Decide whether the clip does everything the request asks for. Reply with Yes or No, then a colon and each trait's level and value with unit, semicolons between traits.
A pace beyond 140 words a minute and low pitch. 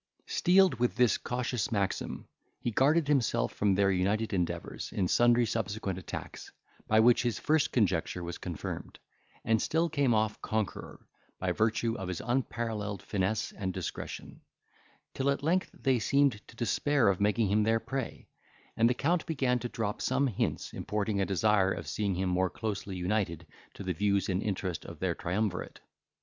Yes: average, 165 wpm; low, 110 Hz